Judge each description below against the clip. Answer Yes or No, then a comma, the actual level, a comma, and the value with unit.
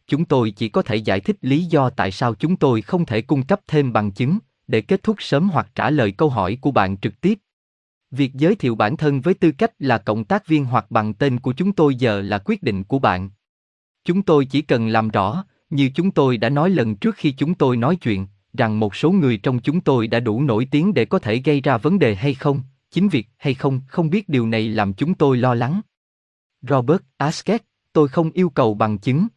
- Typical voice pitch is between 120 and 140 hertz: Yes, low, 135 Hz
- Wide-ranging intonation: Yes, wide, 6.3 semitones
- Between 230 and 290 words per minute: Yes, average, 235 wpm